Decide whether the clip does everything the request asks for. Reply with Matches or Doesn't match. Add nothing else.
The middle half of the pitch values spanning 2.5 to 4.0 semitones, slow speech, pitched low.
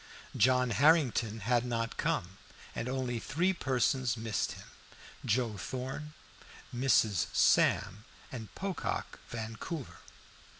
Matches